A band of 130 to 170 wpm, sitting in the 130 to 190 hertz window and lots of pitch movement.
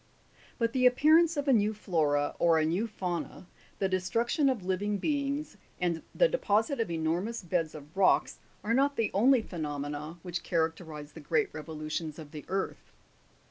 Yes: average, 165 wpm; medium, 185 Hz; wide, 6.6 semitones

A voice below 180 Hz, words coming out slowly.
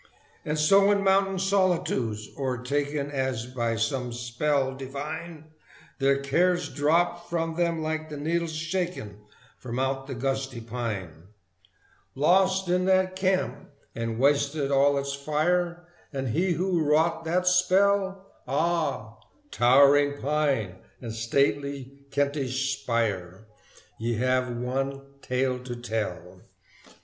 Yes: medium, 140 Hz; slow, 120 wpm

